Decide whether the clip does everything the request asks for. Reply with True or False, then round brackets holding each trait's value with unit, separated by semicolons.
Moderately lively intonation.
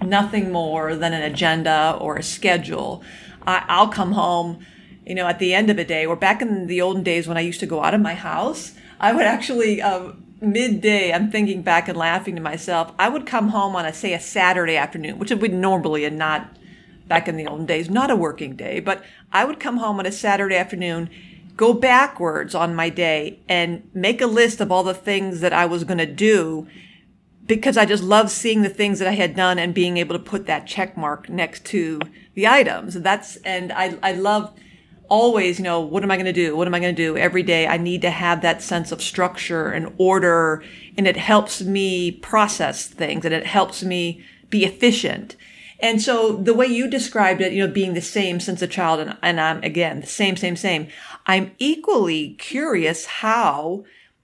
True (3.4 semitones)